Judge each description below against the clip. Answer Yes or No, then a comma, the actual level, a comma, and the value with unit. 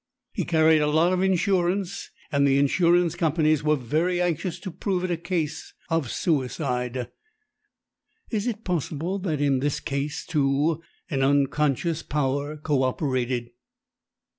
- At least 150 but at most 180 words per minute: No, average, 140 wpm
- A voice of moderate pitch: Yes, medium, 155 Hz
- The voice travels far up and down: No, average, 4.1 semitones